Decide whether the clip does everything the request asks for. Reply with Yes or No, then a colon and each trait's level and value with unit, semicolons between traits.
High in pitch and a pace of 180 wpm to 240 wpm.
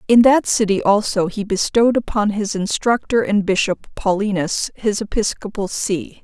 No: high, 210 Hz; average, 145 wpm